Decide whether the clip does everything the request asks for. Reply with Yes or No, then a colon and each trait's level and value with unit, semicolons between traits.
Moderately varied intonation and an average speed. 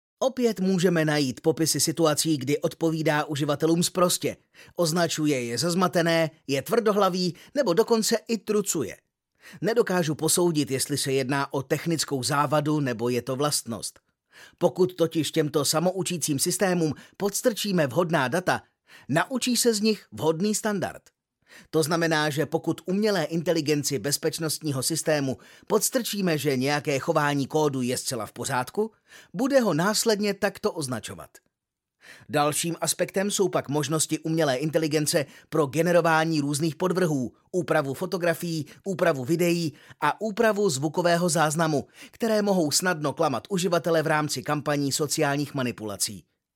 Yes: average, 3.8 semitones; average, 125 wpm